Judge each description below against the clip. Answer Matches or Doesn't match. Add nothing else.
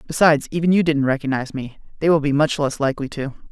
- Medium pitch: Matches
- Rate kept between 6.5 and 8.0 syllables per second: Matches